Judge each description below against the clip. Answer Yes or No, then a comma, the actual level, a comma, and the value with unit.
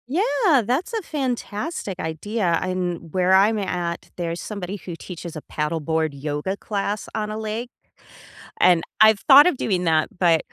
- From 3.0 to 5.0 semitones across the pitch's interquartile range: Yes, average, 4.6 semitones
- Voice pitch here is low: No, high, 190 Hz